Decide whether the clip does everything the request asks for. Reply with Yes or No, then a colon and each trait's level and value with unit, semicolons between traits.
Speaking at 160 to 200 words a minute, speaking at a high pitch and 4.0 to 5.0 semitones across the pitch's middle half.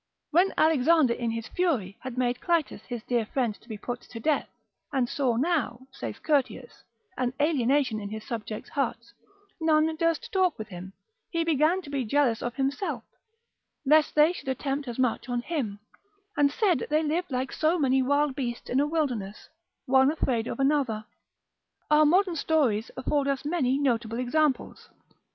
Yes: average, 170 wpm; very high, 270 Hz; average, 4.3 semitones